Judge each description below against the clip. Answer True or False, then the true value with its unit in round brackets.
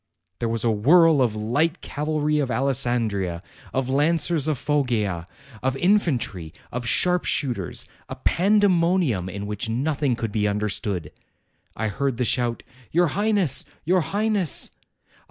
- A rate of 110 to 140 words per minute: True (135 wpm)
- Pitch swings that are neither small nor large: False (7.0 semitones)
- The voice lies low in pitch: True (130 Hz)